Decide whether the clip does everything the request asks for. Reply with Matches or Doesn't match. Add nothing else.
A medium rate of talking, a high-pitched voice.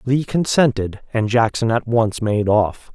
Doesn't match